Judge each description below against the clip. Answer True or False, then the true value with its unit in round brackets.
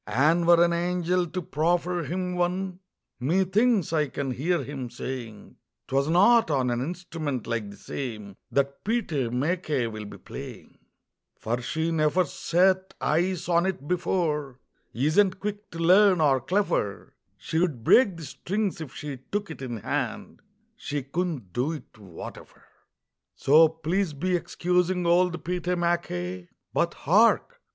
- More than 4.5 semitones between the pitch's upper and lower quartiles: True (5.0 semitones)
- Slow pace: False (145 wpm)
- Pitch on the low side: False (165 Hz)